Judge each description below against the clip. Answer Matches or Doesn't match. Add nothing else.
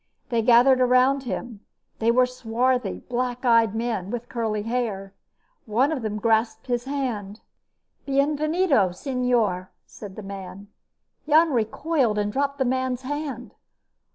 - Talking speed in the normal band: Doesn't match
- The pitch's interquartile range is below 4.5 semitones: Matches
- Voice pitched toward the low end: Doesn't match